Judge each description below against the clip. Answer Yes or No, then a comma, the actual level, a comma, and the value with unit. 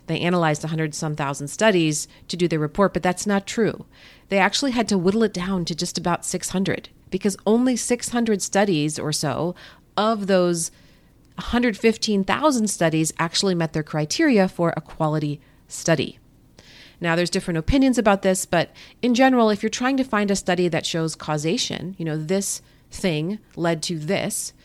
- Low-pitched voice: No, medium, 180 Hz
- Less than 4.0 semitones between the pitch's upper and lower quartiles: No, average, 4.4 semitones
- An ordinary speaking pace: Yes, average, 170 wpm